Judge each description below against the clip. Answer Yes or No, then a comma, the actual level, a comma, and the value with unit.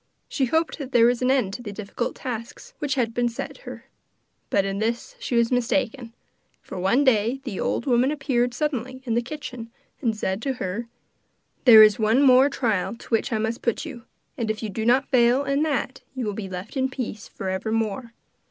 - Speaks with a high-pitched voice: Yes, high, 240 Hz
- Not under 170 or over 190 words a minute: No, fast, 205 wpm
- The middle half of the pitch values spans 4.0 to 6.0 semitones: No, average, 3.1 semitones